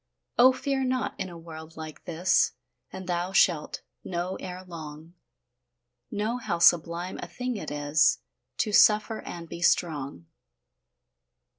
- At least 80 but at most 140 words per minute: Yes, slow, 135 wpm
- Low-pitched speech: No, medium, 175 Hz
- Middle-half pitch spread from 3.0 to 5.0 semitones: Yes, average, 4.3 semitones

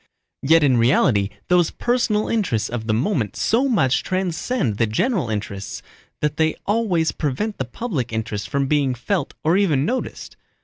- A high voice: No, medium, 150 Hz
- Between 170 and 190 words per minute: No, average, 160 wpm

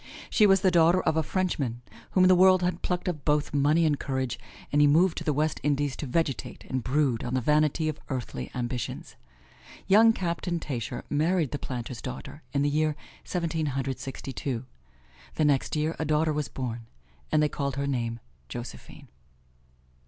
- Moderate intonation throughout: Yes, average, 3.7 semitones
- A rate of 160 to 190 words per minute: Yes, average, 180 wpm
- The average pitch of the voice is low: No, medium, 150 Hz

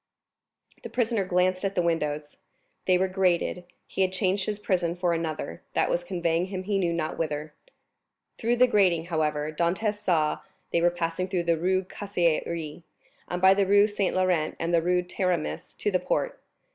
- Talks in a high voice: No, medium, 180 Hz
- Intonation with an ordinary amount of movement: No, narrow, 2.3 semitones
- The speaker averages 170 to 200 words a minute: Yes, average, 175 wpm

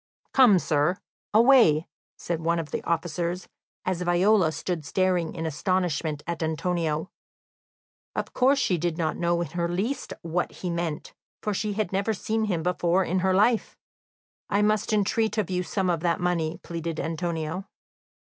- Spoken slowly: No, average, 160 wpm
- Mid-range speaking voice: Yes, medium, 175 Hz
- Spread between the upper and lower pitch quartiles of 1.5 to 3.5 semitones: Yes, average, 2.8 semitones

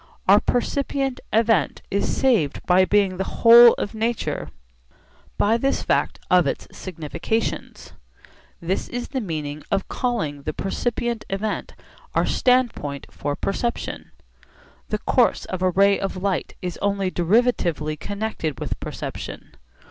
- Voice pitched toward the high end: Yes, high, 200 Hz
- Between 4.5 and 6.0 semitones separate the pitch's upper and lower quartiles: Yes, average, 5.3 semitones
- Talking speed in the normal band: No, slow, 130 wpm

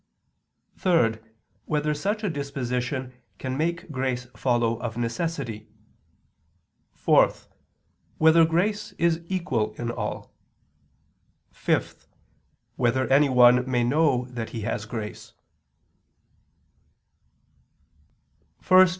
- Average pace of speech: No, slow, 85 wpm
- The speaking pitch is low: Yes, low, 130 Hz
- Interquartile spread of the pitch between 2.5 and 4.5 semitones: No, average, 5.1 semitones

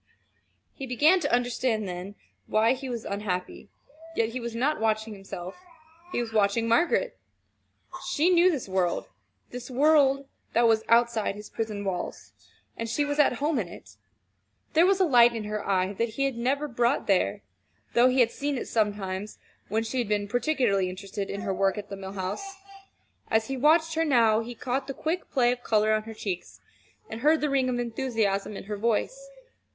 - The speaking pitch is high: Yes, high, 230 Hz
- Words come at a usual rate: Yes, average, 190 wpm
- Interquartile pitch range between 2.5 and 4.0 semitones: No, average, 4.6 semitones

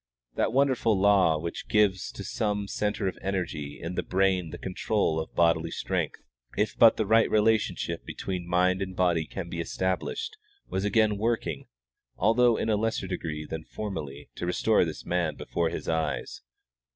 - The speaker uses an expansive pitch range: No, average, 4.1 semitones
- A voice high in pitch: No, very low, 95 Hz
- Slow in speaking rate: No, average, 165 wpm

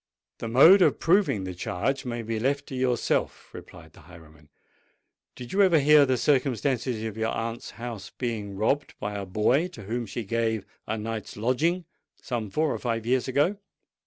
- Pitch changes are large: No, average, 4.2 semitones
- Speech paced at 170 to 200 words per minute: Yes, average, 180 wpm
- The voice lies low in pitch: Yes, low, 120 Hz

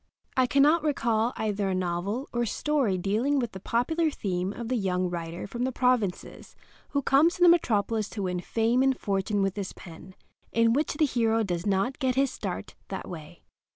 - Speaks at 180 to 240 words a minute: Yes, average, 195 wpm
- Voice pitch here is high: Yes, high, 225 Hz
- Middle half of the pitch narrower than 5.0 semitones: No, average, 5.3 semitones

